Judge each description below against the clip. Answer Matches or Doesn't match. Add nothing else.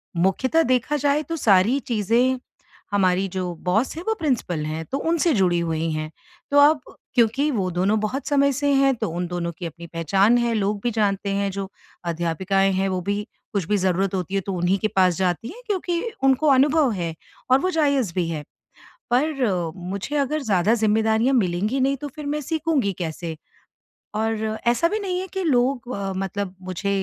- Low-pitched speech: Doesn't match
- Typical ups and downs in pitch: Doesn't match